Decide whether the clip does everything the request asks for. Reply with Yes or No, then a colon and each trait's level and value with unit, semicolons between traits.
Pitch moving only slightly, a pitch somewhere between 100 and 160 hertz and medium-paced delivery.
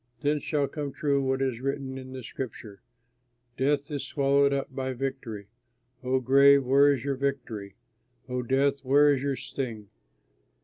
Yes: narrow, 1.5 semitones; low, 135 Hz; average, 150 wpm